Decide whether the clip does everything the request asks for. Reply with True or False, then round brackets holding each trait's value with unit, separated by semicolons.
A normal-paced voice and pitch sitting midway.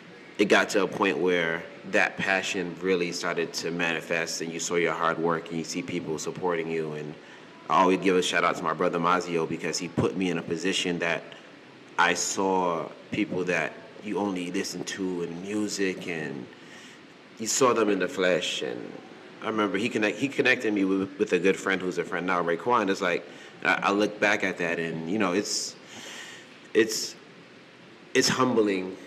False (190 wpm; 90 Hz)